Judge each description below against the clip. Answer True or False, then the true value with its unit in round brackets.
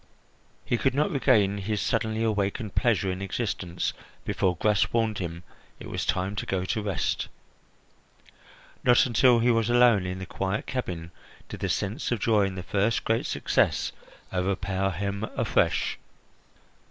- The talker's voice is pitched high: False (100 Hz)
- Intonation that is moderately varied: True (3.3 semitones)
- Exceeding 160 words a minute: False (155 wpm)